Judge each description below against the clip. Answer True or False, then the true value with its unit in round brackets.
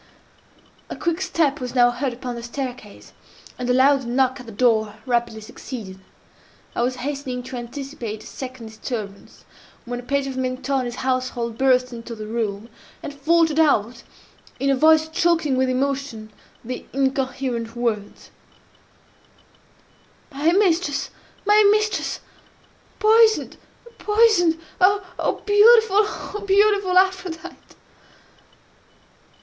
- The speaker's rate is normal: False (110 wpm)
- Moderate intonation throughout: False (5.7 semitones)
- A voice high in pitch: True (265 Hz)